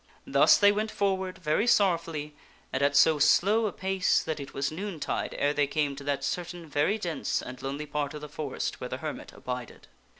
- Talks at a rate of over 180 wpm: Yes, average, 200 wpm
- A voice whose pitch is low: No, medium, 155 Hz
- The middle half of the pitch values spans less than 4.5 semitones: No, average, 4.8 semitones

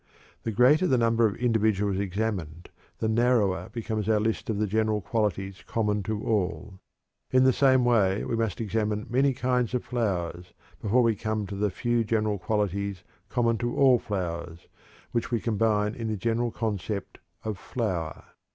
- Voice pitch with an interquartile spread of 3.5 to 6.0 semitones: No, average, 2.7 semitones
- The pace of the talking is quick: No, average, 165 wpm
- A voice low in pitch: Yes, low, 110 Hz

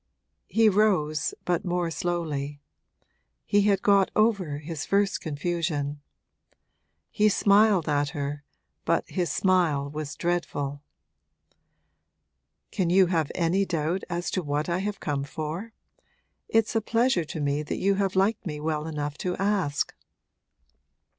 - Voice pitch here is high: No, medium, 175 Hz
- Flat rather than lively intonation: No, average, 4.8 semitones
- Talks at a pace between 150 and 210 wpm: No, slow, 135 wpm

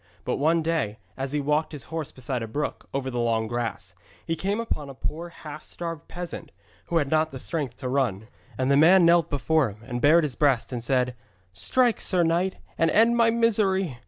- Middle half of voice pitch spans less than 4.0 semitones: No, average, 4.9 semitones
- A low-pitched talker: No, medium, 150 Hz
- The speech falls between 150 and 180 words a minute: No, fast, 205 wpm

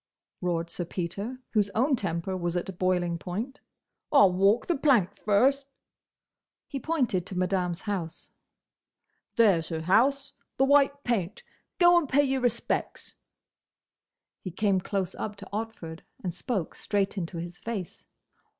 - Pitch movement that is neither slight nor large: No, wide, 5.7 semitones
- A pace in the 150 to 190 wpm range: No, average, 140 wpm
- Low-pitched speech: No, high, 200 Hz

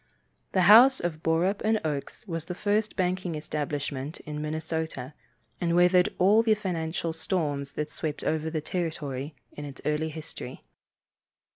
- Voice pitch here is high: No, medium, 160 Hz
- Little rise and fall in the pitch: No, average, 3.2 semitones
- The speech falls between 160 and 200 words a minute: No, average, 145 wpm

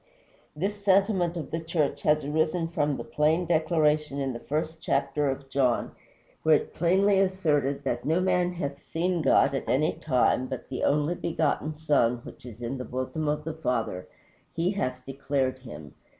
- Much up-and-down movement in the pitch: No, average, 3.7 semitones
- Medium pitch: Yes, medium, 150 Hz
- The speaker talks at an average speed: Yes, average, 180 wpm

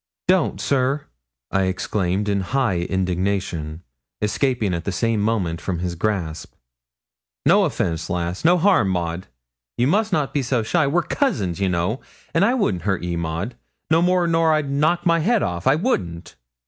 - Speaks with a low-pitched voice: Yes, low, 105 Hz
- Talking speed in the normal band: Yes, average, 170 wpm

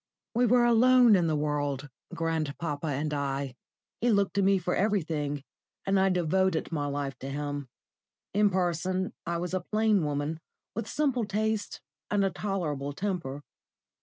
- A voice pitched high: No, medium, 175 Hz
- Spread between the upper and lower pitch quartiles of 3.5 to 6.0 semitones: Yes, wide, 5.6 semitones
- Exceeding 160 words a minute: No, average, 155 wpm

